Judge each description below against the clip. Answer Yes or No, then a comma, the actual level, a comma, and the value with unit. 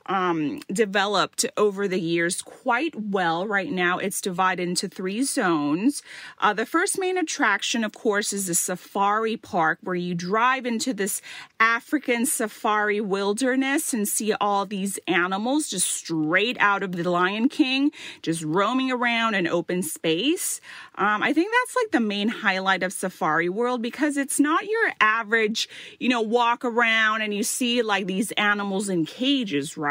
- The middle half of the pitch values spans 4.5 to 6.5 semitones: Yes, average, 5.2 semitones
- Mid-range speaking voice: No, high, 215 Hz